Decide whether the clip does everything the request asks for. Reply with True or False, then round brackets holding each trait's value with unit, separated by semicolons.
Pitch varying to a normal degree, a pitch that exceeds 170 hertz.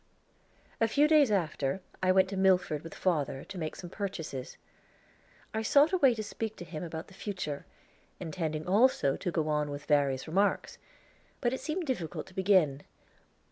False (5.8 semitones; 185 Hz)